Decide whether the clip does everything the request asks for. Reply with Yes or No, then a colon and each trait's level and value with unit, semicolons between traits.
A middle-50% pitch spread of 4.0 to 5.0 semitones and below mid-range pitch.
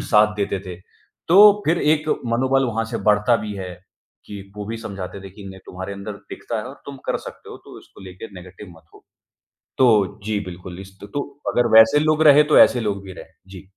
Yes: average, 4.6 semitones; low, 105 Hz